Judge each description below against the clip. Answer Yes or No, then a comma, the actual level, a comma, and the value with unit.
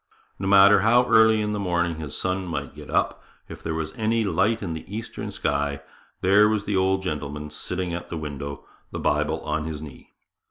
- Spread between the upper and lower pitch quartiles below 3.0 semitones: No, average, 5.1 semitones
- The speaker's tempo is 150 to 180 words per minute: No, average, 200 wpm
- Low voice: Yes, very low, 95 Hz